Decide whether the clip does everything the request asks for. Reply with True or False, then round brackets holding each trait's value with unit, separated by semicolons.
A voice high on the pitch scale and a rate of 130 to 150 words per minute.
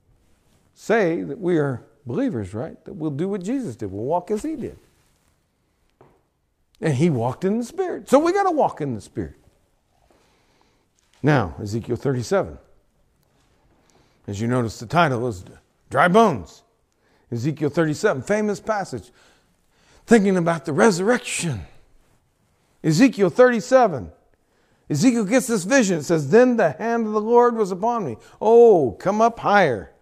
False (180 Hz; 140 wpm)